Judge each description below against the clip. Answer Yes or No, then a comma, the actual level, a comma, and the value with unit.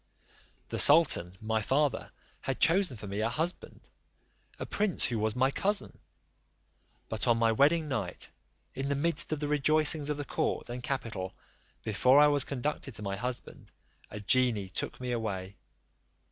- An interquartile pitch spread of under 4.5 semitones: No, average, 5.3 semitones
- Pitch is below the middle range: Yes, low, 130 Hz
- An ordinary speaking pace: Yes, average, 160 wpm